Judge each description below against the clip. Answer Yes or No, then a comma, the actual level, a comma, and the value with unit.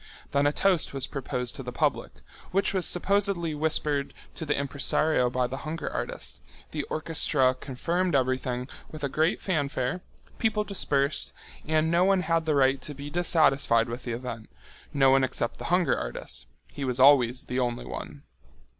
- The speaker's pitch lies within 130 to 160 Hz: Yes, medium, 140 Hz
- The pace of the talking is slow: No, average, 165 wpm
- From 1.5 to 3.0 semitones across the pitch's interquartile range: No, average, 4.2 semitones